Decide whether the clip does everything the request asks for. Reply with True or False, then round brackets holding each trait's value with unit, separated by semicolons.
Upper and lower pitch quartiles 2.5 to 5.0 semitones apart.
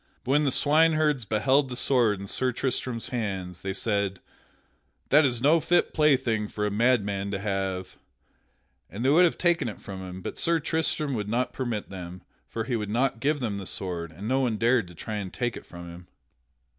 False (5.5 semitones)